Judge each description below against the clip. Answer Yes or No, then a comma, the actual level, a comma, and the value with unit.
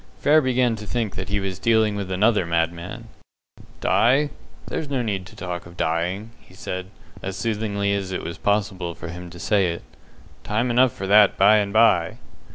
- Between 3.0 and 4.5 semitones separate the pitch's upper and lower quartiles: Yes, average, 3.6 semitones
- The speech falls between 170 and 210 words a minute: Yes, average, 185 wpm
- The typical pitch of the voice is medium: No, low, 100 Hz